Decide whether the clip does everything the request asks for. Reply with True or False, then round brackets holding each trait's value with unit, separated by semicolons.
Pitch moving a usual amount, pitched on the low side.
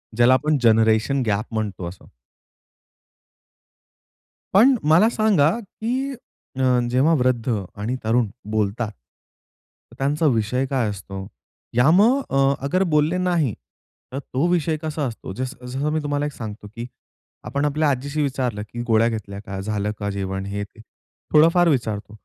False (5.8 semitones; 130 Hz)